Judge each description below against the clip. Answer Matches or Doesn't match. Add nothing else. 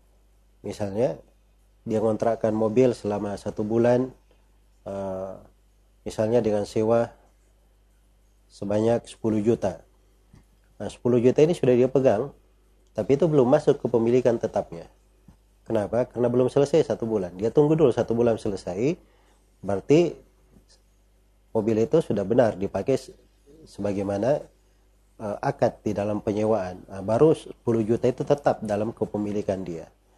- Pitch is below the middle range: Matches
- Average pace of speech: Matches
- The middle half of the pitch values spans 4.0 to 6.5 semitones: Doesn't match